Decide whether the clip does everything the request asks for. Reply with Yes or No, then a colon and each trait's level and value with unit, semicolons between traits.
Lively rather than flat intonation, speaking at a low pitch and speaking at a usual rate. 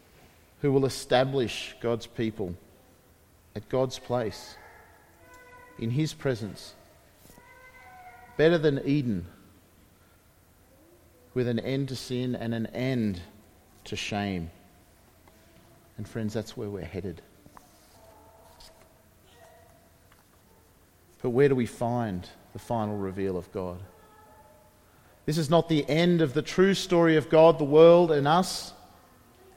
No: wide, 7.6 semitones; low, 115 Hz; slow, 110 wpm